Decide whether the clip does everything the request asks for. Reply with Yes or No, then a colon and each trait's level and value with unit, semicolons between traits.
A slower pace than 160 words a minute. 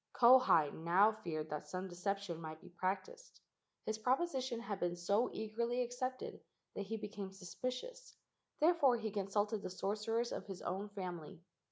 Yes: average, 150 wpm